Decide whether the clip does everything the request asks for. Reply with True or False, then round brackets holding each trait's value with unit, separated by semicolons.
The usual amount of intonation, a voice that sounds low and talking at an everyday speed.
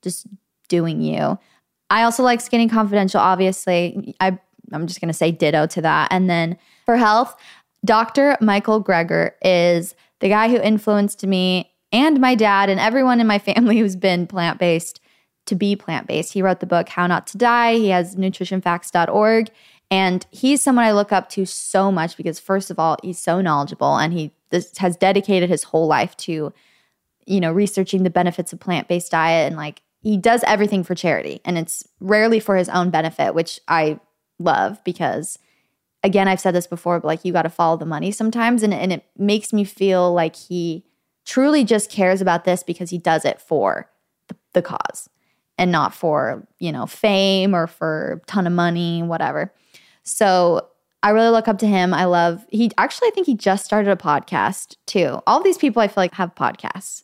False (3.6 semitones; 185 Hz; 190 wpm)